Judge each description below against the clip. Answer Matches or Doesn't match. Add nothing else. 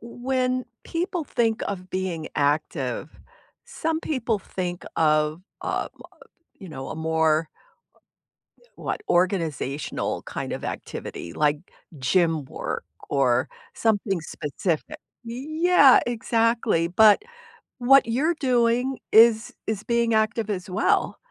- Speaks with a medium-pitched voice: Doesn't match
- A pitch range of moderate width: Doesn't match